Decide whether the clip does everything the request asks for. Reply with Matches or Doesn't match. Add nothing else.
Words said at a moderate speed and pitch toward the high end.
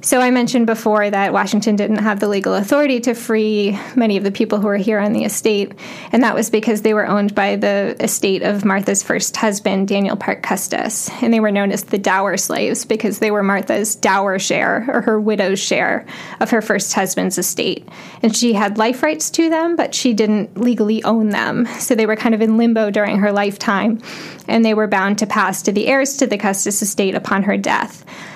Doesn't match